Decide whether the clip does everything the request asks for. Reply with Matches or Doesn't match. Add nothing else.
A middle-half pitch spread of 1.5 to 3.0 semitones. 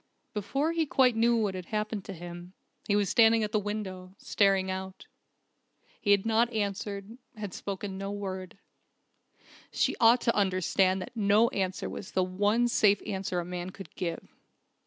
Matches